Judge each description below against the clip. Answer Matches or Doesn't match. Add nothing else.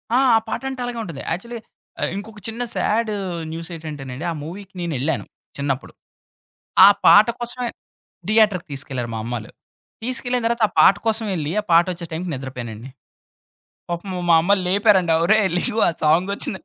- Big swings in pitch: Matches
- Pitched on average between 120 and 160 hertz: Doesn't match